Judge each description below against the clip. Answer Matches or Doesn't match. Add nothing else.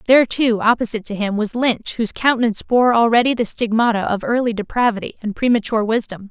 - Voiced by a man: Doesn't match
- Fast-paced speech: Doesn't match